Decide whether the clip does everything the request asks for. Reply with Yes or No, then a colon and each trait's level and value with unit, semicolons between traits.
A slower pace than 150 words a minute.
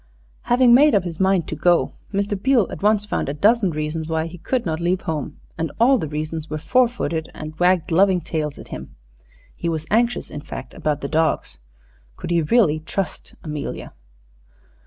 No: average, 190 wpm